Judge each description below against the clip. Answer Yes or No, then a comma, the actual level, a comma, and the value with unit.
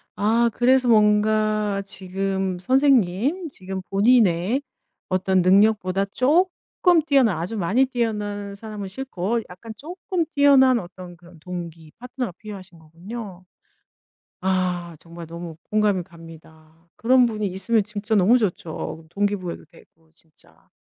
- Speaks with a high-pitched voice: Yes, high, 200 Hz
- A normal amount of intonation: Yes, average, 4.7 semitones